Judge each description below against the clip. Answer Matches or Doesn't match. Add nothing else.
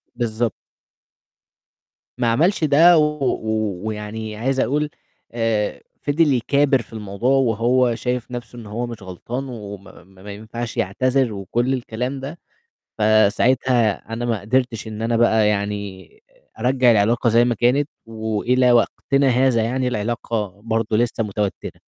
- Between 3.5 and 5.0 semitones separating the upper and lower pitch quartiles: Doesn't match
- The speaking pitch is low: Matches